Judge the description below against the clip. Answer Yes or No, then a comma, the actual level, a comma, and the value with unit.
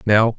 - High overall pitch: No, low, 110 Hz